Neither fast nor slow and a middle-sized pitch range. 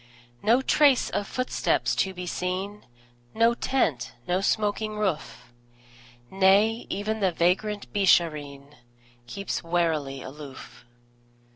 No: slow, 105 wpm; average, 4.6 semitones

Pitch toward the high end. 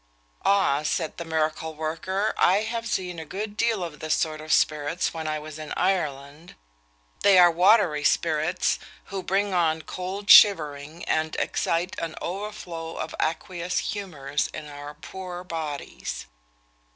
No: medium, 165 Hz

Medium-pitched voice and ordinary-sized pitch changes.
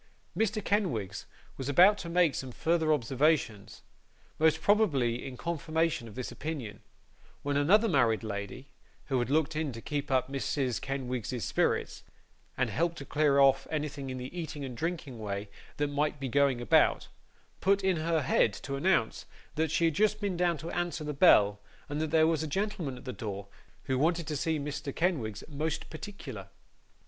Yes: medium, 145 Hz; average, 4.4 semitones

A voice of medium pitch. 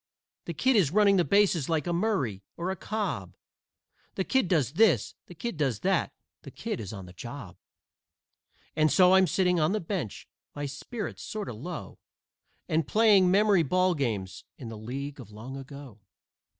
Yes: medium, 160 Hz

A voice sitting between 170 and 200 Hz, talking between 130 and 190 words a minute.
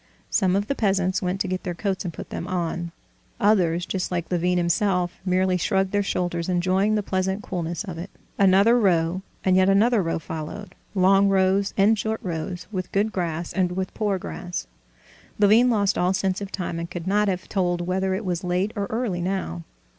Yes: medium, 185 Hz; average, 185 wpm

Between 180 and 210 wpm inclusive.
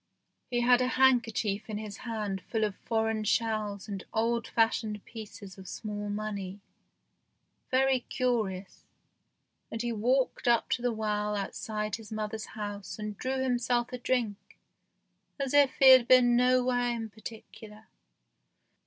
No: average, 140 wpm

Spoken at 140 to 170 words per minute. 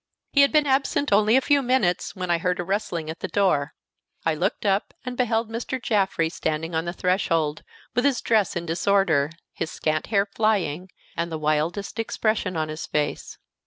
No: average, 190 wpm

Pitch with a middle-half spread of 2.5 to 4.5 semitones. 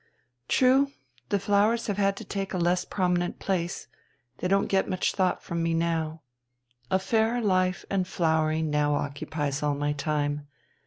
Yes: average, 4.1 semitones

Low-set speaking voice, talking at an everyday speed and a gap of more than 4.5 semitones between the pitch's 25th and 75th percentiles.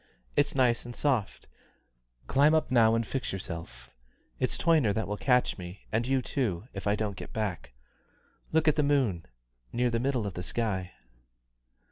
Yes: low, 115 Hz; average, 170 wpm; average, 4.9 semitones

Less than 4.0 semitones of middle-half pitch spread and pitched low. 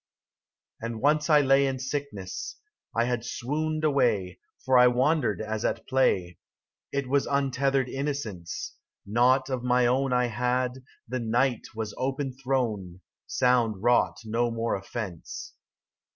Yes: average, 3.0 semitones; low, 125 Hz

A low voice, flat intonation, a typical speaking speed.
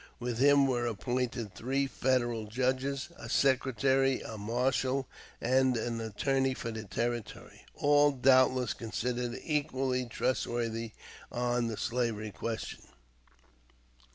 No: low, 125 Hz; narrow, 2.3 semitones; slow, 110 wpm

